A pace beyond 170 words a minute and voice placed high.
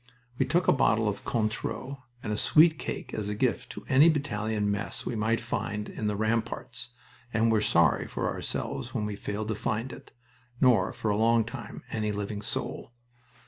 No: average, 185 wpm; low, 110 Hz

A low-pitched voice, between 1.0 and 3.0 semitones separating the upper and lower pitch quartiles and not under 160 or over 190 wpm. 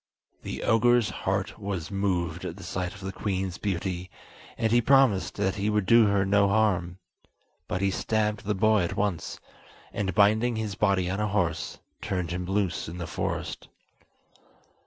Yes: low, 100 Hz; average, 2.7 semitones; average, 170 wpm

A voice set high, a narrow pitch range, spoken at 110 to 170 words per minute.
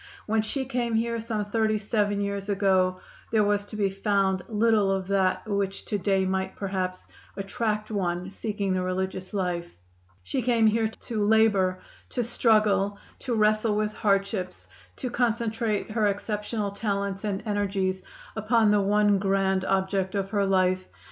Yes: high, 205 Hz; narrow, 2.1 semitones; average, 155 wpm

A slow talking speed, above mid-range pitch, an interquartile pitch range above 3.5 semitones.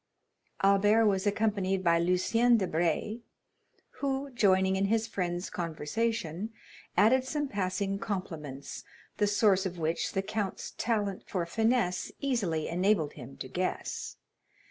Yes: slow, 120 wpm; high, 195 Hz; average, 3.9 semitones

